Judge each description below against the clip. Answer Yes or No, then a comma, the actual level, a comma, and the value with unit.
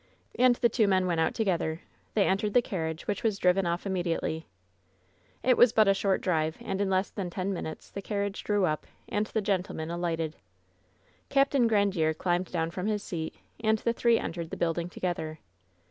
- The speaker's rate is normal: Yes, average, 190 wpm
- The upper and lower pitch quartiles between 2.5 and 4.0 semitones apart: Yes, average, 3.6 semitones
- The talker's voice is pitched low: No, high, 190 Hz